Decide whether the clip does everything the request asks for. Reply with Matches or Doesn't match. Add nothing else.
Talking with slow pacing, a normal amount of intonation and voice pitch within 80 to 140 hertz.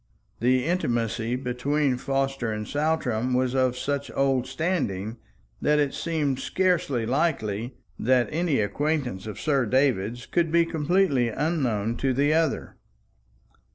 Matches